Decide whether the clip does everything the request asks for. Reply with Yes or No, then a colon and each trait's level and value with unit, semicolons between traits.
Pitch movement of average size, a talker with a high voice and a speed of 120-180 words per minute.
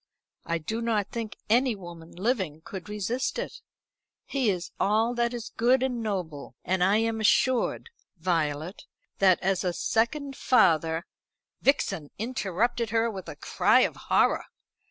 Yes: average, 5.0 semitones; high, 210 Hz; average, 150 wpm